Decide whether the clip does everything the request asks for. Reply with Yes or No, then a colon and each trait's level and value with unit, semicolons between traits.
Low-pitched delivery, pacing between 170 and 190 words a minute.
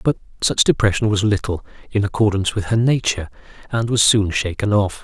Yes: low, 105 Hz; average, 180 wpm